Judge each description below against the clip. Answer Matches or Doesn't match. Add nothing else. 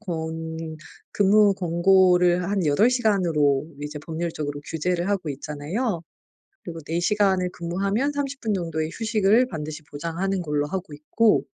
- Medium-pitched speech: Matches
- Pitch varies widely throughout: Doesn't match